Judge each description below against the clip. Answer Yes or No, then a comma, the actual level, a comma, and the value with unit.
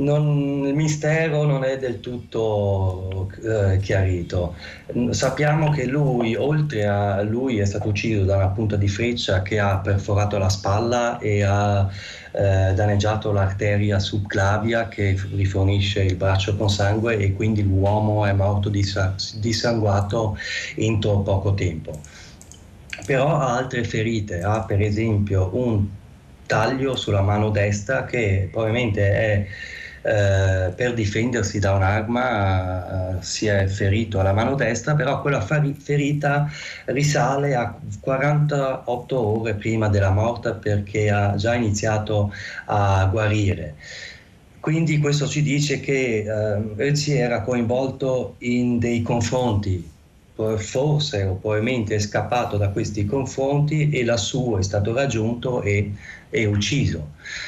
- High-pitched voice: No, low, 105 Hz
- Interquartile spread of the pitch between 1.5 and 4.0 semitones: Yes, average, 3.7 semitones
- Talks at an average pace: Yes, average, 125 wpm